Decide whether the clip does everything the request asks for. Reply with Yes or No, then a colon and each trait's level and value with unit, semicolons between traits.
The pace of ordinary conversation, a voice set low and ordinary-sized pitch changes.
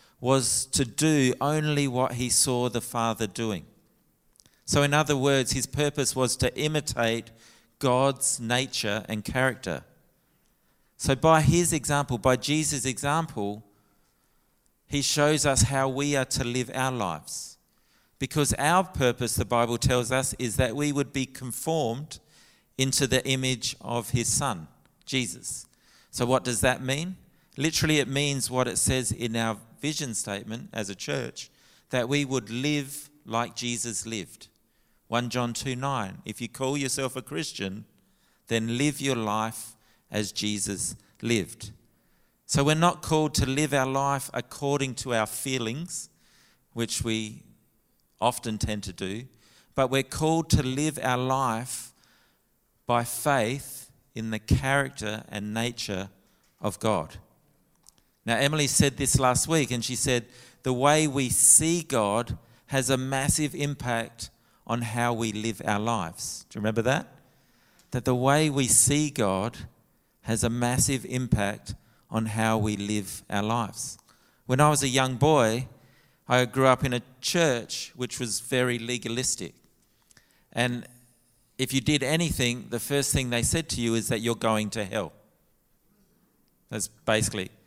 Yes: average, 150 wpm; low, 125 Hz; average, 3.4 semitones